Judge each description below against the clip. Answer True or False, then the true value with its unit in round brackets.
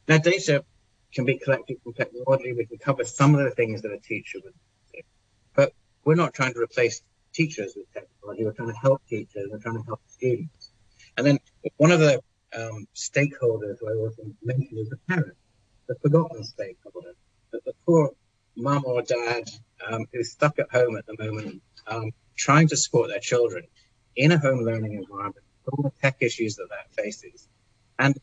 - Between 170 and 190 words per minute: True (185 wpm)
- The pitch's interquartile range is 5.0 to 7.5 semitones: False (4.5 semitones)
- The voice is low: True (120 Hz)